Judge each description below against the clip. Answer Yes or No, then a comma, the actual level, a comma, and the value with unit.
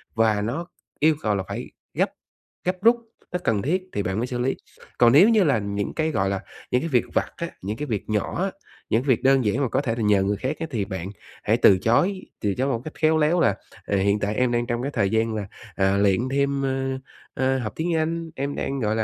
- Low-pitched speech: Yes, low, 125 Hz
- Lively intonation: Yes, wide, 6.4 semitones